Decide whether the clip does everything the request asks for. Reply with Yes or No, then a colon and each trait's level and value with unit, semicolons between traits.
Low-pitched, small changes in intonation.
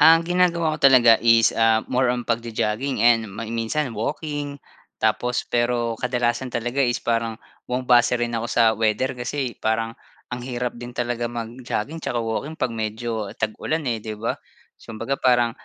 Yes: low, 120 Hz; narrow, 2.1 semitones